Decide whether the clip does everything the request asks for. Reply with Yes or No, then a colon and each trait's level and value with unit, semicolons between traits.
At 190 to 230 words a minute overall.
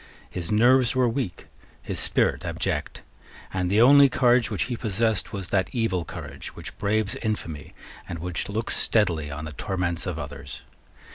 No: average, 160 wpm